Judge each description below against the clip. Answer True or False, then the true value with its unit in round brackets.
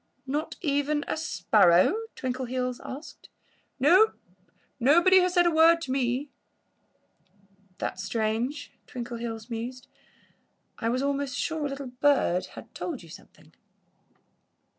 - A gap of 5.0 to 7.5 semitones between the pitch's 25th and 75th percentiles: False (4.0 semitones)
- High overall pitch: True (265 Hz)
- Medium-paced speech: False (120 wpm)